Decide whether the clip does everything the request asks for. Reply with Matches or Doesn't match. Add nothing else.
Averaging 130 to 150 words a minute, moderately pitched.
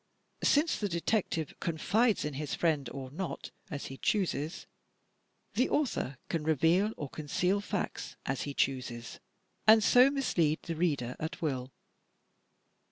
Matches